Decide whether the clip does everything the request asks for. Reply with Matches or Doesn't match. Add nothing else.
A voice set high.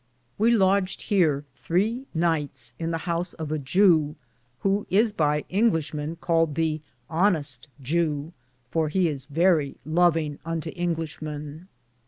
Doesn't match